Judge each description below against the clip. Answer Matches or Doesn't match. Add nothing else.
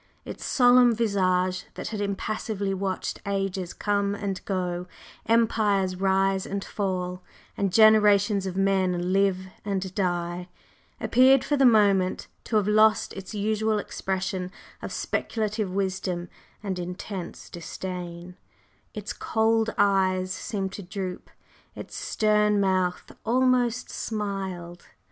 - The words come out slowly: Matches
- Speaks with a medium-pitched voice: Doesn't match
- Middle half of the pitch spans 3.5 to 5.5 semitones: Doesn't match